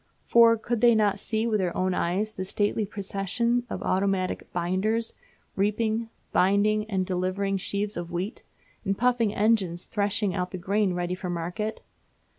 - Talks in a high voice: Yes, high, 200 Hz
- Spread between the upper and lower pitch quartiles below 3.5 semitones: Yes, average, 2.8 semitones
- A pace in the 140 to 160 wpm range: Yes, average, 155 wpm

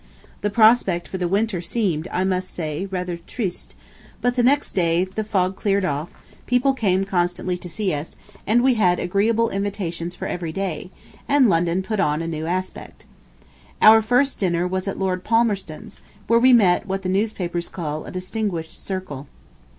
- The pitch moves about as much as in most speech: Yes, average, 3.7 semitones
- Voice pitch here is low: No, high, 190 Hz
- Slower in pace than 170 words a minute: No, average, 175 wpm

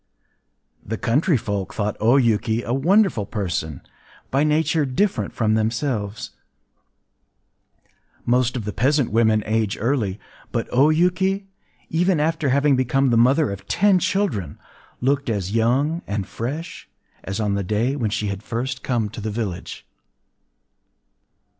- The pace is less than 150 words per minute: Yes, average, 140 wpm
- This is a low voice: Yes, low, 120 Hz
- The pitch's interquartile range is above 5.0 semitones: Yes, wide, 5.4 semitones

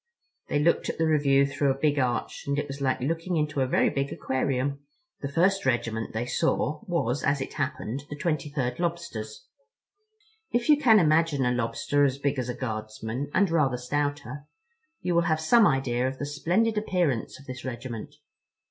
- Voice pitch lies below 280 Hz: Yes, medium, 140 Hz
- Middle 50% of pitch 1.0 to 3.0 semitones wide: No, average, 3.7 semitones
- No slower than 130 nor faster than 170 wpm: No, average, 185 wpm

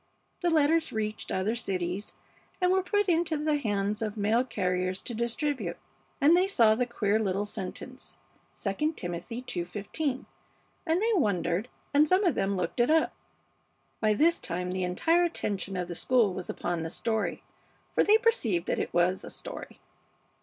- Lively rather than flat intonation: Yes, wide, 8.6 semitones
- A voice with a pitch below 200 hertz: No, high, 220 Hz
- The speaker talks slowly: No, average, 165 wpm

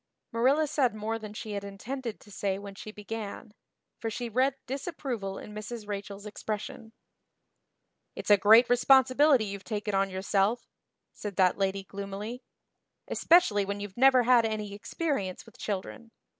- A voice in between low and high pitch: No, high, 215 Hz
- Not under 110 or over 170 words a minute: Yes, average, 150 wpm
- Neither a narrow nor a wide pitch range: Yes, average, 3.4 semitones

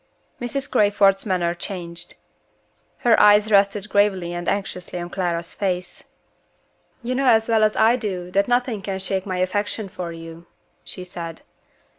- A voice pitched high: Yes, high, 195 Hz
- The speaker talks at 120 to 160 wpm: Yes, average, 150 wpm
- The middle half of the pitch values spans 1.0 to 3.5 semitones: Yes, average, 3.0 semitones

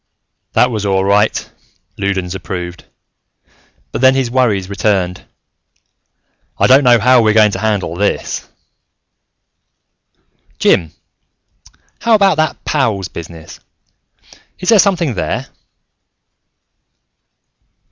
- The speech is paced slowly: Yes, slow, 105 wpm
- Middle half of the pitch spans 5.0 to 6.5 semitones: Yes, wide, 5.5 semitones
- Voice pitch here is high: No, low, 105 Hz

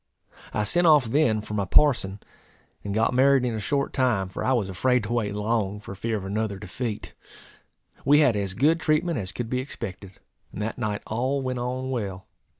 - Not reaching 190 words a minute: No, average, 200 wpm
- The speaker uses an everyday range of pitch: Yes, average, 4.2 semitones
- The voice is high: No, low, 115 Hz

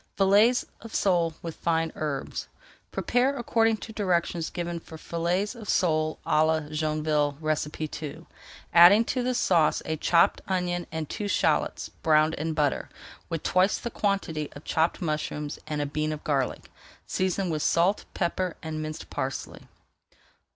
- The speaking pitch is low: No, medium, 165 Hz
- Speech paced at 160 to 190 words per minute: No, average, 150 wpm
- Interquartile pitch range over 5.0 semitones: No, average, 3.6 semitones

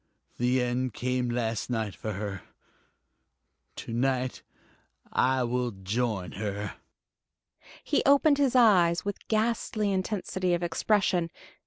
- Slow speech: Yes, slow, 115 wpm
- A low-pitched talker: Yes, low, 125 Hz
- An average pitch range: No, wide, 8.7 semitones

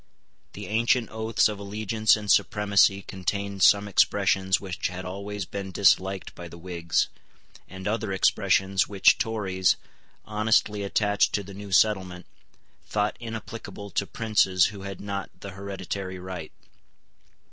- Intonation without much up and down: Yes, narrow, 1.7 semitones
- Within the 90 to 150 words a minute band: Yes, slow, 135 wpm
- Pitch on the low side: Yes, low, 100 Hz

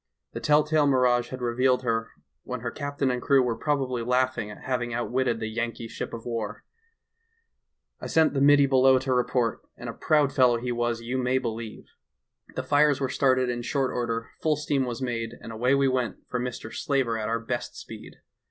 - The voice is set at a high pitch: No, low, 125 Hz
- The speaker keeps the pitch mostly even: Yes, narrow, 2.3 semitones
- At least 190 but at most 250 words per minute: Yes, average, 200 wpm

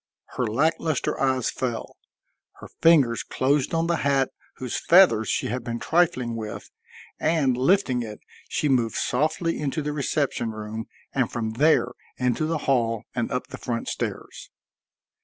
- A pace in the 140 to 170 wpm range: Yes, average, 155 wpm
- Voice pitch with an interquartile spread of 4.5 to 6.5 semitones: Yes, average, 4.8 semitones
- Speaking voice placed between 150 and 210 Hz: No, low, 130 Hz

